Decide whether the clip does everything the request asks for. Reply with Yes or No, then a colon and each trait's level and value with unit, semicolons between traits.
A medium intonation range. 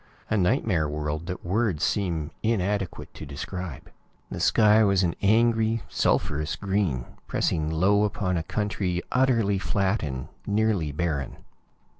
Yes: average, 4.8 semitones